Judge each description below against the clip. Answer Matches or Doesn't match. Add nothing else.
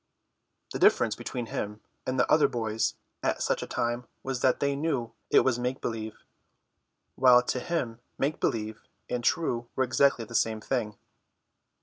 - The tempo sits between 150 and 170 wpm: Matches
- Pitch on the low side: Matches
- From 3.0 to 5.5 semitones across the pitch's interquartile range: Doesn't match